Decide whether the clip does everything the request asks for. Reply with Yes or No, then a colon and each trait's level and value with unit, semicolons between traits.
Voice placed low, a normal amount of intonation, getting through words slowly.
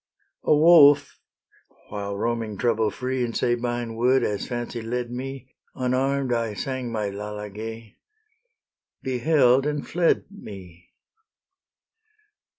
Yes: low, 120 Hz; average, 3.2 semitones; slow, 105 wpm